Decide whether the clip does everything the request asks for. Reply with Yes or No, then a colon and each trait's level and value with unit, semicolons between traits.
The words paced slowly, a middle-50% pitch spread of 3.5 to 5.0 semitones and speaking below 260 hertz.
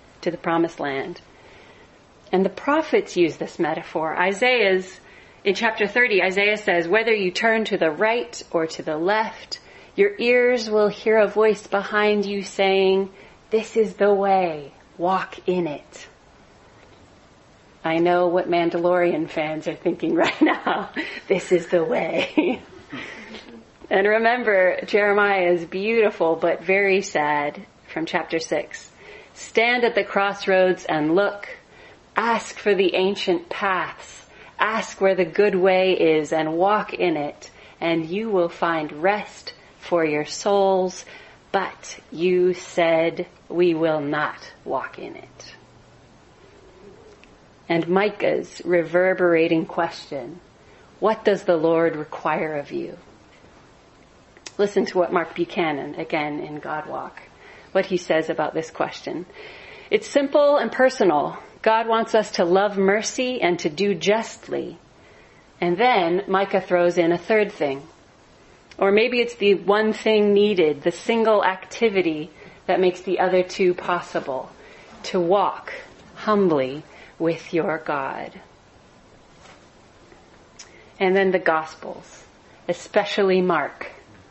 Yes: slow, 130 wpm; average, 3.8 semitones; medium, 185 Hz